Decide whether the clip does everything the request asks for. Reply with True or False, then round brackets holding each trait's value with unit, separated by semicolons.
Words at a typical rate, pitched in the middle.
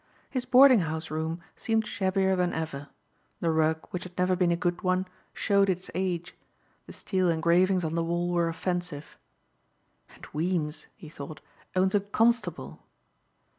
True (155 wpm; 175 Hz)